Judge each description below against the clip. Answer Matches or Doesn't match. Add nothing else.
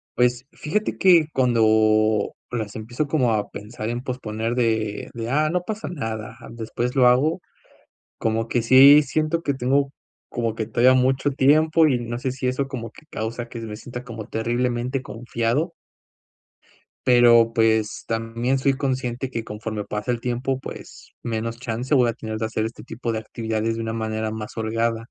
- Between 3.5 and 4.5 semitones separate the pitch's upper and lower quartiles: Doesn't match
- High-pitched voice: Doesn't match